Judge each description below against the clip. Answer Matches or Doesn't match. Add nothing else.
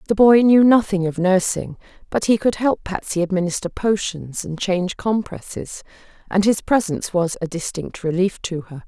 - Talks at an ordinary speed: Matches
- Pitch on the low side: Doesn't match